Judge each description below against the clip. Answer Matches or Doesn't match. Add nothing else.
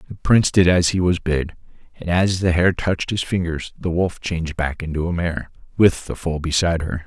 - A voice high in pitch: Doesn't match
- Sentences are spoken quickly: Matches